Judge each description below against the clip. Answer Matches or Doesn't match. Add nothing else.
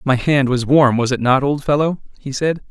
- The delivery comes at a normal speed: Doesn't match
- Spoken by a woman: Doesn't match